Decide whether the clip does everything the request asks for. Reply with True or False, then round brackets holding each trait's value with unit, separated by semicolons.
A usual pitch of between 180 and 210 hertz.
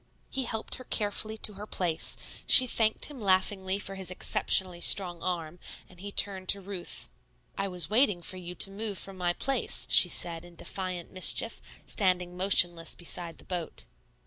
True (185 Hz)